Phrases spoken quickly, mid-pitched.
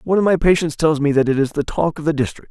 Yes: fast, 335 wpm; medium, 155 Hz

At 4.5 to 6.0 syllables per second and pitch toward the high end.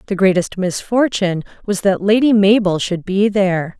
Yes: 5.0 syllables/s; high, 195 Hz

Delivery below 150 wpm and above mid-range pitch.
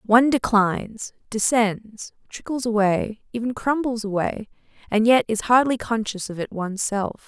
Yes: average, 140 wpm; high, 225 Hz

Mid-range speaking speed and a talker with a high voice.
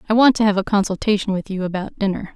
No: fast, 255 wpm; high, 200 Hz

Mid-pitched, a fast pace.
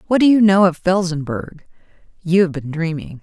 No: medium, 175 Hz; average, 185 wpm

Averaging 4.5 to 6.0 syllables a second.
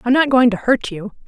Yes: 5.6 syllables/s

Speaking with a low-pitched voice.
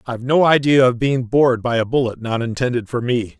Yes: low, 125 Hz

